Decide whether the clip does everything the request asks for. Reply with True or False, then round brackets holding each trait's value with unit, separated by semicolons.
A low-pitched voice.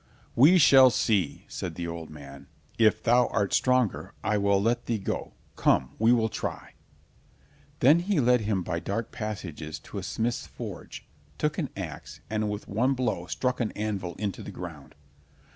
True (110 Hz)